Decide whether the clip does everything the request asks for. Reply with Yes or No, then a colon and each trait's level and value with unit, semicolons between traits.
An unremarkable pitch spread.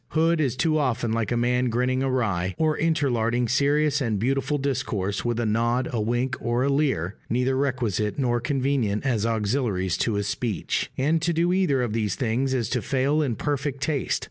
Yes: average, 3.7 semitones